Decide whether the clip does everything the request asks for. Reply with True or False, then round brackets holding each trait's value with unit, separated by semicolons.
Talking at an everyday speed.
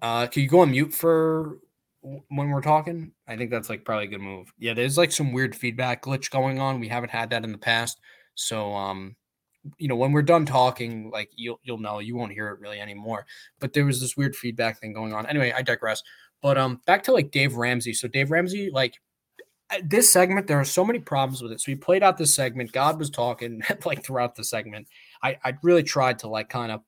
False (235 wpm)